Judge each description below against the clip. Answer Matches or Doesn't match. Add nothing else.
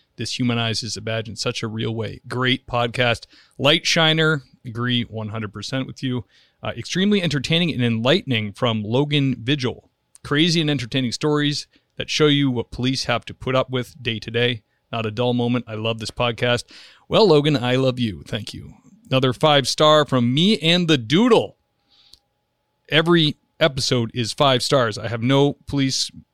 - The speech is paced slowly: Doesn't match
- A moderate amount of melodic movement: Matches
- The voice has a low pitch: Matches